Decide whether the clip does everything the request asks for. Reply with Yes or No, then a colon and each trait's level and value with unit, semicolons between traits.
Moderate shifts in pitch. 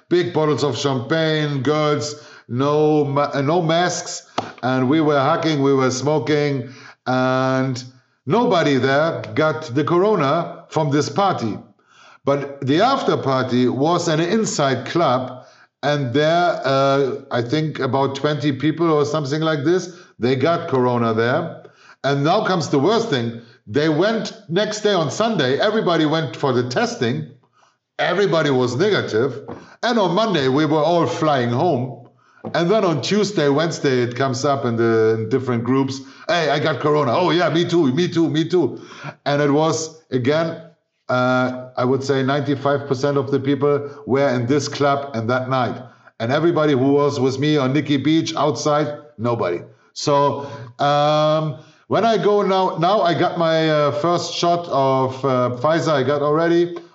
Yes: average, 3.3 semitones